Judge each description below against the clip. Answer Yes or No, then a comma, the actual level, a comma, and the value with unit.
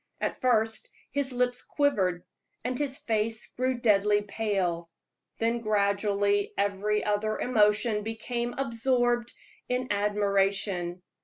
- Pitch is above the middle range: Yes, high, 215 Hz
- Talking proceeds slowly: Yes, slow, 105 wpm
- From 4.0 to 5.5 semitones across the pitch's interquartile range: No, average, 3.2 semitones